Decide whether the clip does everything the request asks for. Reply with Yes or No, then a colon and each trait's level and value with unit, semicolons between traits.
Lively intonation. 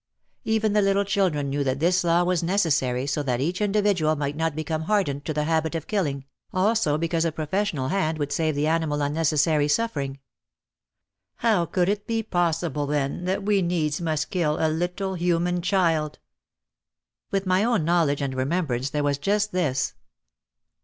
No: average, 4.2 semitones